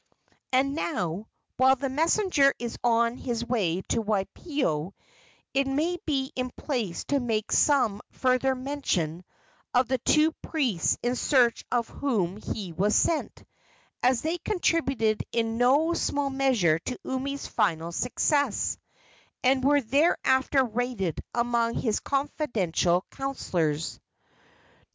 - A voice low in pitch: No, very high, 250 Hz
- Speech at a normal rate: No, slow, 125 wpm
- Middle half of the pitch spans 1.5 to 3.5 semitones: No, average, 4.4 semitones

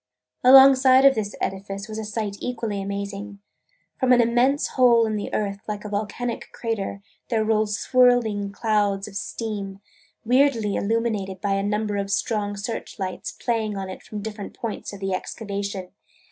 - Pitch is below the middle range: No, high, 210 Hz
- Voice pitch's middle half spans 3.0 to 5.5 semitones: No, narrow, 2.6 semitones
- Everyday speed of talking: Yes, average, 160 wpm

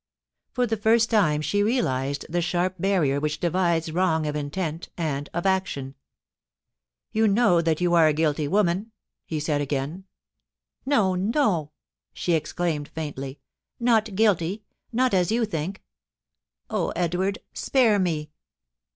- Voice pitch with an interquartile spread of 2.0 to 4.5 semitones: No, average, 5.0 semitones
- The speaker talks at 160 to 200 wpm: No, average, 150 wpm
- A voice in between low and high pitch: Yes, medium, 175 Hz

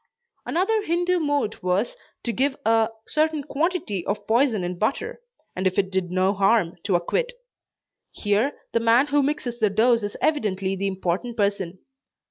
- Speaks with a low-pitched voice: No, high, 220 Hz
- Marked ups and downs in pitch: Yes, wide, 6.9 semitones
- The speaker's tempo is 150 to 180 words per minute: Yes, average, 160 wpm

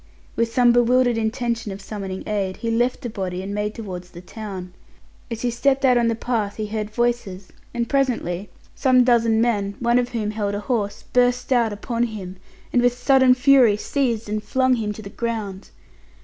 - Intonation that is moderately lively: Yes, average, 3.1 semitones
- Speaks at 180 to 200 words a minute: Yes, average, 190 wpm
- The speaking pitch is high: Yes, high, 230 Hz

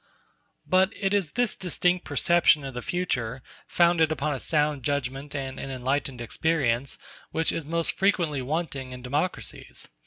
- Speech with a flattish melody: No, average, 4.5 semitones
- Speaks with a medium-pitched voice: Yes, medium, 150 Hz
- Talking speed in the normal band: Yes, average, 150 wpm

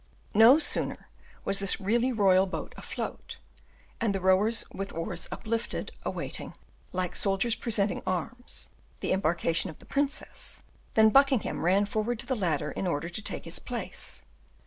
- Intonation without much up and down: No, average, 3.8 semitones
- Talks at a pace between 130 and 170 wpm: Yes, average, 150 wpm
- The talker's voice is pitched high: Yes, high, 200 Hz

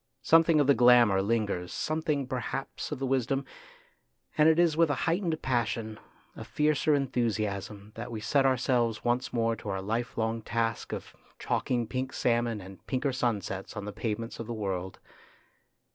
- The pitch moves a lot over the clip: No, average, 4.0 semitones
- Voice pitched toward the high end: No, low, 120 Hz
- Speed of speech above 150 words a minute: Yes, average, 170 wpm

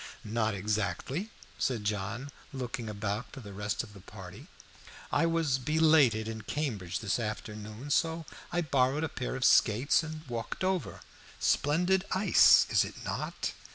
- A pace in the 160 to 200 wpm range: No, average, 150 wpm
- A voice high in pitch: No, low, 125 Hz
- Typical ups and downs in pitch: No, wide, 6.4 semitones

